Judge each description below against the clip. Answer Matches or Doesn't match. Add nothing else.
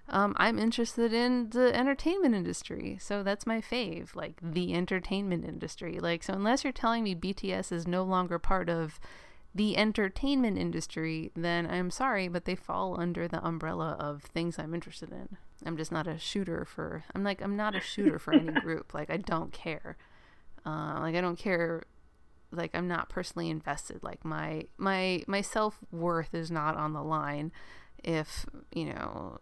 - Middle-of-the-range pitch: Matches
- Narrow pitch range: Doesn't match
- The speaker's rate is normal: Matches